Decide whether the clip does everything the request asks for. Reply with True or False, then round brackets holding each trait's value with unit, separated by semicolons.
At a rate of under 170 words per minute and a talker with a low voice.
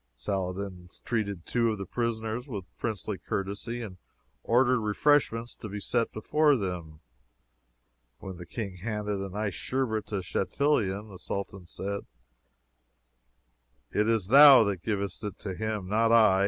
True (140 wpm; 105 Hz)